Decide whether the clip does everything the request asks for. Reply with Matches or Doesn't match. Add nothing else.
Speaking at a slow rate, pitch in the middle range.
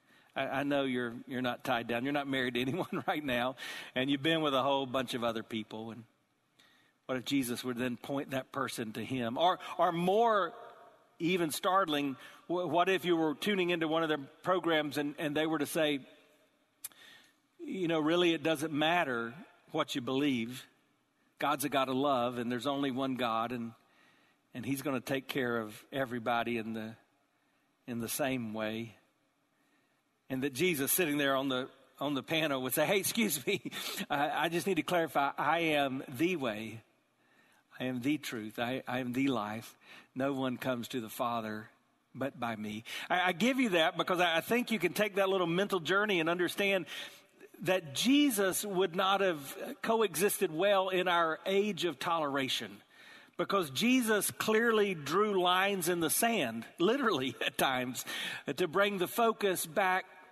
Doesn't match